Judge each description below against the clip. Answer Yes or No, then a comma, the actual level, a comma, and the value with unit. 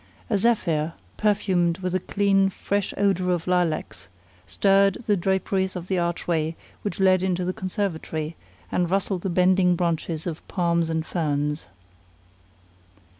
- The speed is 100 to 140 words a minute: Yes, slow, 135 wpm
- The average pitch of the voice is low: No, medium, 180 Hz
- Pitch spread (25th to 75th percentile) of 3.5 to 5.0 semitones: No, narrow, 2.4 semitones